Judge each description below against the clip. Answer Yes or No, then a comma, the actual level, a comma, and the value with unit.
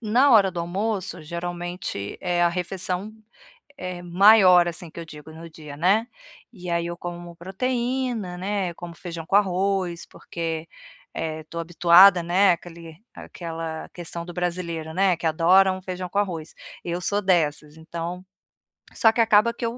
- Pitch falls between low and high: Yes, medium, 175 Hz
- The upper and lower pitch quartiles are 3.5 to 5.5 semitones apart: No, narrow, 2.4 semitones